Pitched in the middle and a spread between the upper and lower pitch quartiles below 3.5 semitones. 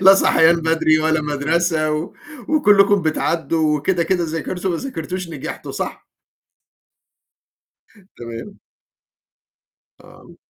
Yes: medium, 165 Hz; average, 2.9 semitones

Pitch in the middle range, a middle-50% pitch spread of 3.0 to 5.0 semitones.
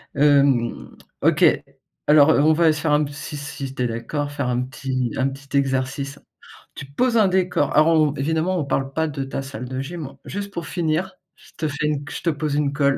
No: medium, 145 Hz; narrow, 2.5 semitones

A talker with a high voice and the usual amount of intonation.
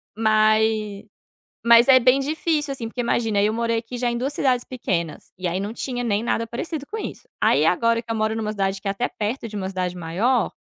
Yes: high, 225 Hz; average, 3.3 semitones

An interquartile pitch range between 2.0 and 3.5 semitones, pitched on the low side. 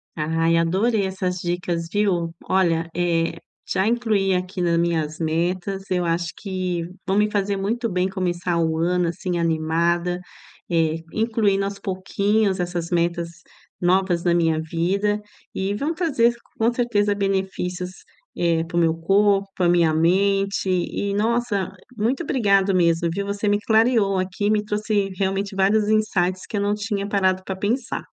No: average, 3.0 semitones; high, 190 Hz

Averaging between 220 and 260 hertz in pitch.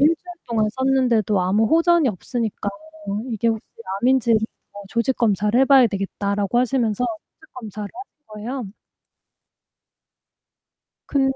Yes: high, 235 Hz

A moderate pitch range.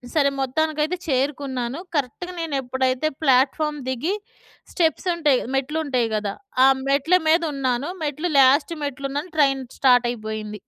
Yes: average, 3.2 semitones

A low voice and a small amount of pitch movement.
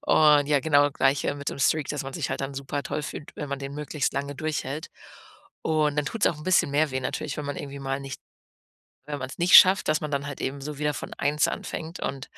No: medium, 145 Hz; narrow, 1.5 semitones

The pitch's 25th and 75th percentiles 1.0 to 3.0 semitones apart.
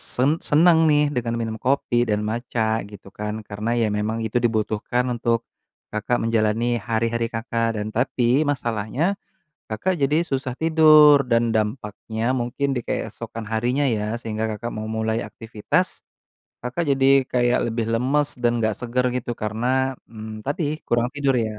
Yes: average, 2.7 semitones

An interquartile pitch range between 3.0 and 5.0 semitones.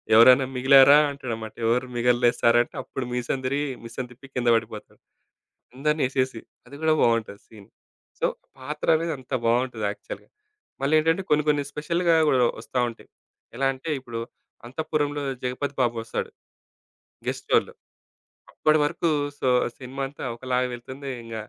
Yes: average, 3.3 semitones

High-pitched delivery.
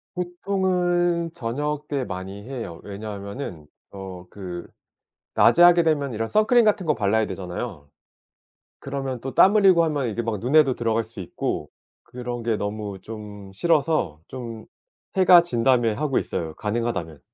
No: low, 120 Hz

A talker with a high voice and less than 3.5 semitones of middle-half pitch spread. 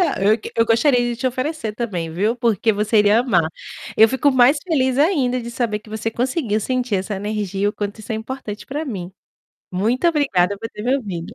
No: high, 225 Hz; average, 3.8 semitones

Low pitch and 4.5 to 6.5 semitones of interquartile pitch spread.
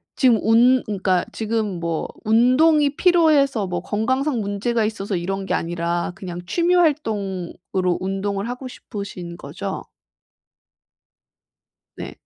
No: high, 205 Hz; wide, 5.5 semitones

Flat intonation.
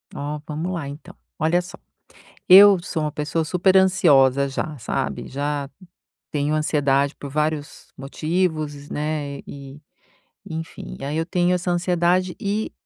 No: average, 3.8 semitones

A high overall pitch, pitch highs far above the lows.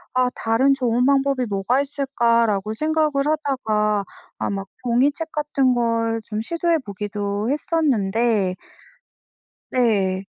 No: high, 240 Hz; average, 4.7 semitones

